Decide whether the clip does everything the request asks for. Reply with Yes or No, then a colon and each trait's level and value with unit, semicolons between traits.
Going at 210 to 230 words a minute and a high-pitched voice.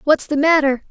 No: average, 200 wpm; very high, 290 Hz